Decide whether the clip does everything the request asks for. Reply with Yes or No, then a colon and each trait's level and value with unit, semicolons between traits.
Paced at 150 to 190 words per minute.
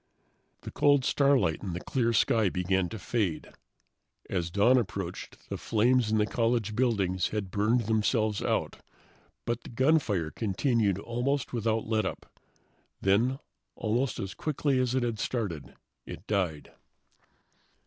No: slow, 135 wpm